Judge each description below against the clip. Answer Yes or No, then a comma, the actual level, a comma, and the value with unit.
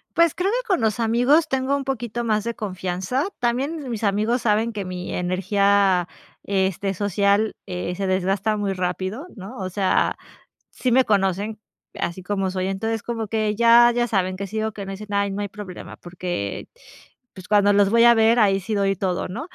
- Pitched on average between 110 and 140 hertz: No, high, 205 Hz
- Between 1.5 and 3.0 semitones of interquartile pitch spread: No, average, 3.5 semitones